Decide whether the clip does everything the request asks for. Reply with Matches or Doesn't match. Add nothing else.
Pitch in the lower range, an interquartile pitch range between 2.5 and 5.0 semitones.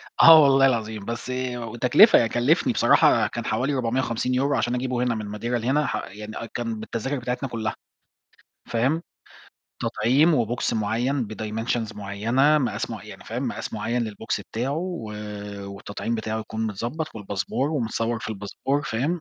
Matches